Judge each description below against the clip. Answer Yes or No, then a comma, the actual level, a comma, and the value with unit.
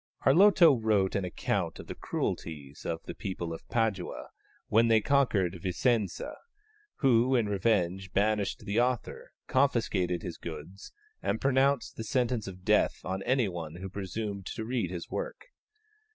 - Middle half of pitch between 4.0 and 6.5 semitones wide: Yes, average, 5.0 semitones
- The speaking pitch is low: Yes, low, 105 Hz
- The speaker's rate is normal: Yes, average, 145 wpm